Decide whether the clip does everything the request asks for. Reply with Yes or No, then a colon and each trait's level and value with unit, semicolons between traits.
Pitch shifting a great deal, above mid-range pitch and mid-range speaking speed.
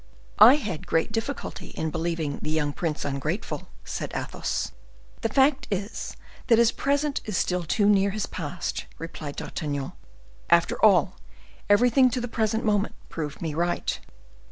Yes: wide, 6.4 semitones; high, 195 Hz; average, 150 wpm